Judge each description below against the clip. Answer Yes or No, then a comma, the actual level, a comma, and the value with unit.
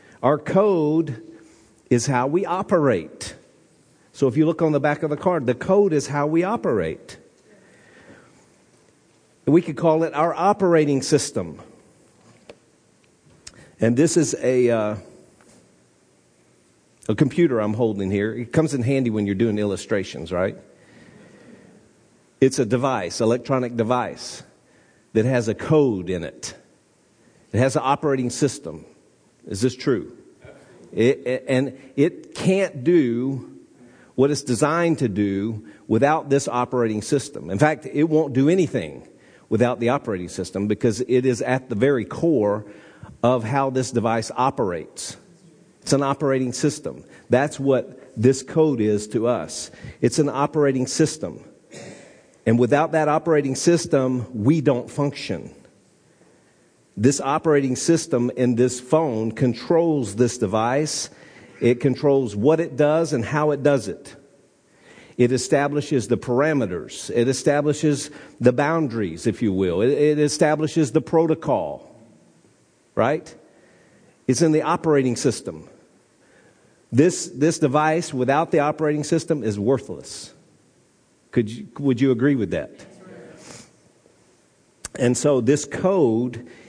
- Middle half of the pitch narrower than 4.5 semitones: Yes, average, 4.0 semitones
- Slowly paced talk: Yes, slow, 130 wpm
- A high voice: No, low, 135 Hz